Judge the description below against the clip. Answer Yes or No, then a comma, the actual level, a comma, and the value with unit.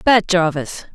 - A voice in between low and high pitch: Yes, medium, 180 Hz